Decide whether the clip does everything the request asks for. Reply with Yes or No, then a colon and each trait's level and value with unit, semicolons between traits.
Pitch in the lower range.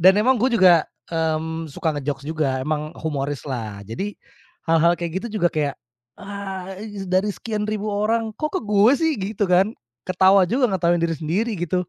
No: medium, 185 Hz